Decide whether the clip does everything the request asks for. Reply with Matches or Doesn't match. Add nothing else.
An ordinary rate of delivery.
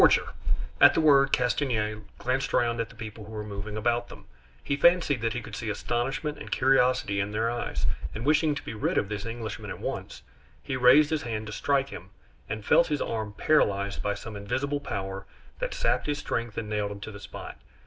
Doesn't match